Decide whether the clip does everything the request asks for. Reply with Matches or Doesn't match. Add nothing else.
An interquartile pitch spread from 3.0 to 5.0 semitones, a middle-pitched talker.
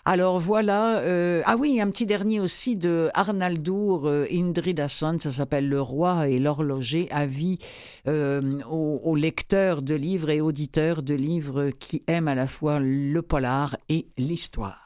Matches